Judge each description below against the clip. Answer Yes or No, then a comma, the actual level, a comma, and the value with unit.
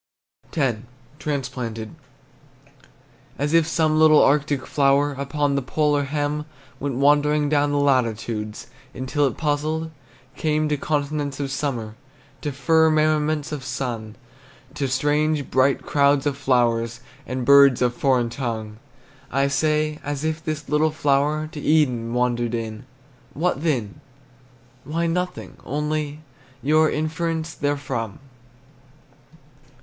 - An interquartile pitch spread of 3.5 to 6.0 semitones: No, average, 2.9 semitones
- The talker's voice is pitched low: No, medium, 145 Hz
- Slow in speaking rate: Yes, slow, 120 wpm